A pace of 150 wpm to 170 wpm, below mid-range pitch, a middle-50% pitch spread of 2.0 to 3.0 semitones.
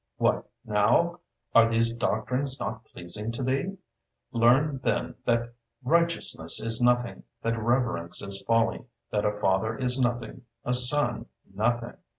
No: slow, 135 wpm; low, 120 Hz; narrow, 2.4 semitones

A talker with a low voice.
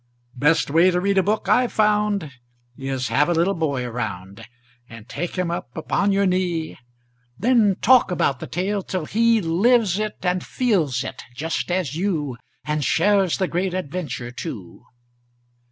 No: medium, 175 Hz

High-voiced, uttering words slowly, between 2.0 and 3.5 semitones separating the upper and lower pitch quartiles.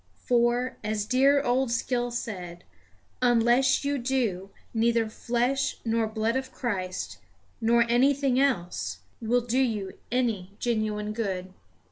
Yes: high, 235 Hz; slow, 120 wpm; average, 3.0 semitones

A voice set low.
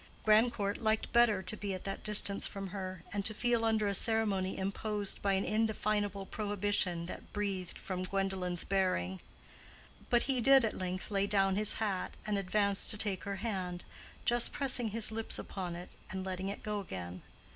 No: high, 200 Hz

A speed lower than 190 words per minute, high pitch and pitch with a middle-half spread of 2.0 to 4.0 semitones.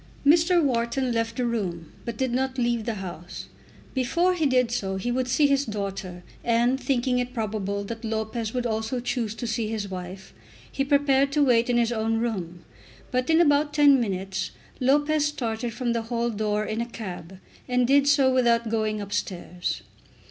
Yes: average, 180 wpm; high, 235 Hz; average, 3.4 semitones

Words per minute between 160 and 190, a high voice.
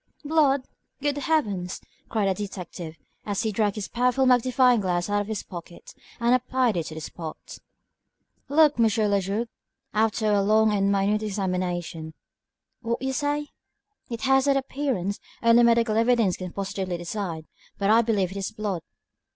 Yes: average, 165 wpm; high, 215 Hz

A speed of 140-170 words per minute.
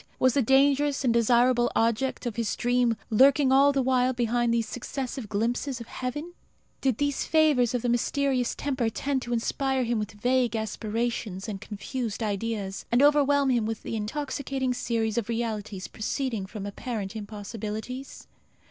Yes: average, 155 wpm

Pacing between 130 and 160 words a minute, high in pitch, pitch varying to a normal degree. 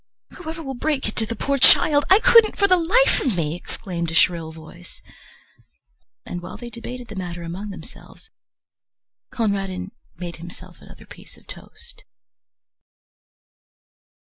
No: average, 145 wpm; high, 205 Hz; wide, 8.2 semitones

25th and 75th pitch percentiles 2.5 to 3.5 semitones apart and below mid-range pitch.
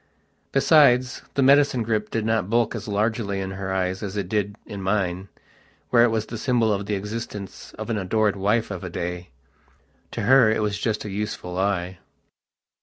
Yes: average, 2.9 semitones; low, 105 Hz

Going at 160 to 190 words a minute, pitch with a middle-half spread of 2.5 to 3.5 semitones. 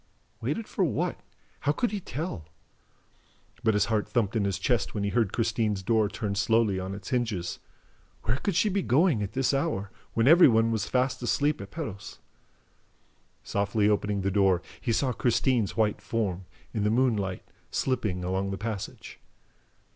No: average, 170 wpm; average, 4.1 semitones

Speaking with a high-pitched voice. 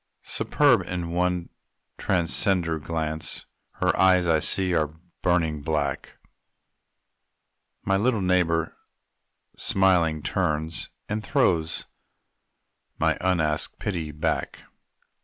No: very low, 85 Hz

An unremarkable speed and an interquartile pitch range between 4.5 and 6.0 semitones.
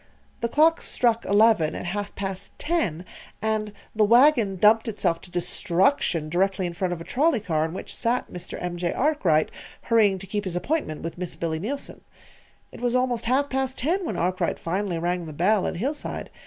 Yes: average, 190 wpm; wide, 5.6 semitones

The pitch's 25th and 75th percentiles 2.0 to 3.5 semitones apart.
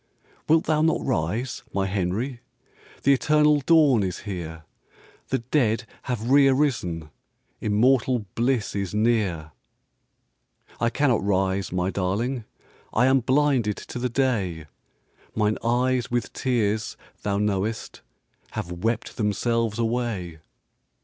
No: average, 4.6 semitones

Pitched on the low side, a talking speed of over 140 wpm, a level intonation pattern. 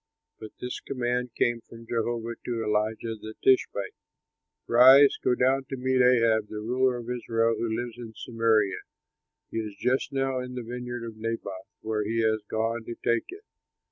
Yes: low, 115 Hz; average, 175 wpm; narrow, 2.0 semitones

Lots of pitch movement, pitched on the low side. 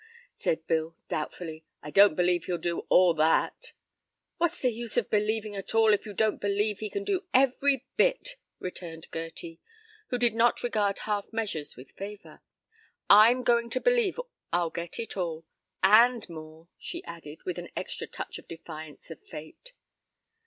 No: wide, 6.3 semitones; high, 205 Hz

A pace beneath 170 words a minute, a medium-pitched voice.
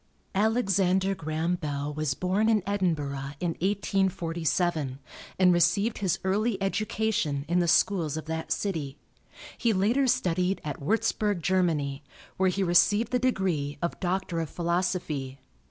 Yes: slow, 135 wpm; medium, 180 Hz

